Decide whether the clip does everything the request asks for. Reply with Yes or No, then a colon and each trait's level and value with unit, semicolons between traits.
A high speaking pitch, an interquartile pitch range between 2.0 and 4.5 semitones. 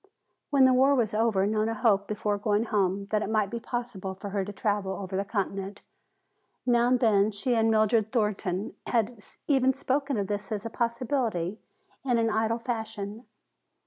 Yes: high, 215 Hz; average, 2.8 semitones